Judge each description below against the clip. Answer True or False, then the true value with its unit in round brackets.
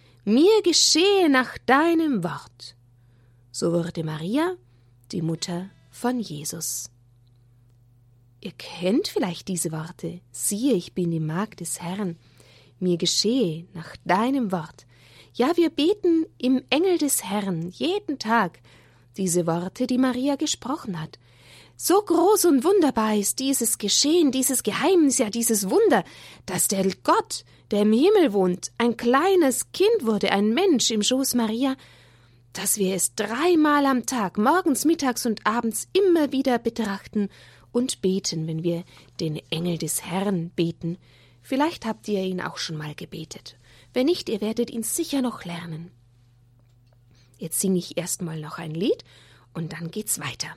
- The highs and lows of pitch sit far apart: True (8.5 semitones)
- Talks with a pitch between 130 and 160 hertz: False (195 Hz)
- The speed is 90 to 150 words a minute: True (145 wpm)